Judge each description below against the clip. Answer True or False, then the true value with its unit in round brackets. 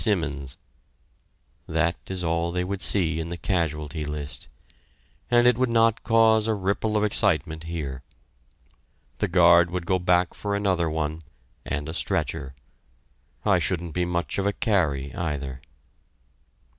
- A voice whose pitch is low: True (85 Hz)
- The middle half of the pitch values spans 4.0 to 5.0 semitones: True (4.3 semitones)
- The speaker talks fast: False (145 wpm)